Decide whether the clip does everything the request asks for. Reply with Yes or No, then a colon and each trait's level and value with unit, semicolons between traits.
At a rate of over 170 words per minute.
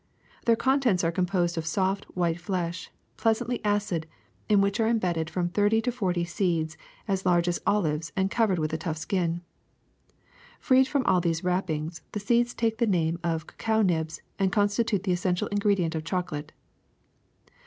No: average, 165 wpm